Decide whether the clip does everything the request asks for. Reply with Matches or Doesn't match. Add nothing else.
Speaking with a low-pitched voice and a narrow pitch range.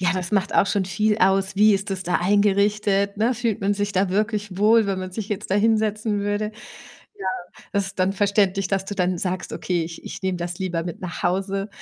Doesn't match